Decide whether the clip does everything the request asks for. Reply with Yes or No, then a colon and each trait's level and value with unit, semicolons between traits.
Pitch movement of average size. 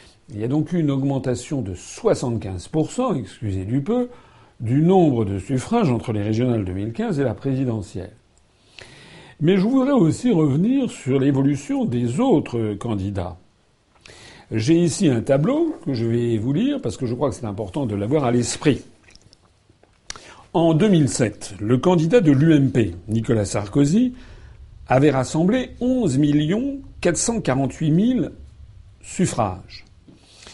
No: wide, 7.1 semitones